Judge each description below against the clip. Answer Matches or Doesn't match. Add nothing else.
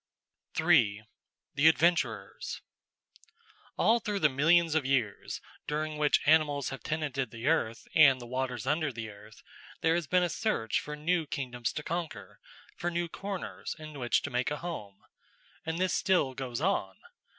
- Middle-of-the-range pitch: Matches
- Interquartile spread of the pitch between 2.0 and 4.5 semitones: Doesn't match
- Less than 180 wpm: Matches